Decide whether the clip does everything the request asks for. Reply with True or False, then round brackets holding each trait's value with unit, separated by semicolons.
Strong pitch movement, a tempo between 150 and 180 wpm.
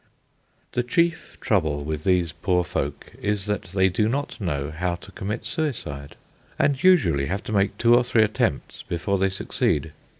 True (6.1 semitones; 170 wpm)